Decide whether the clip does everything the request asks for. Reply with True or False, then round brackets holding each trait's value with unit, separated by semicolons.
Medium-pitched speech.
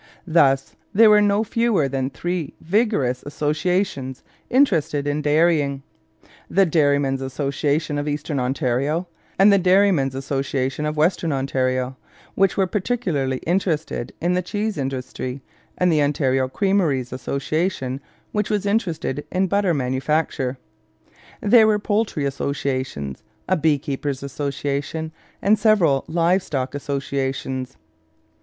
True (150 Hz)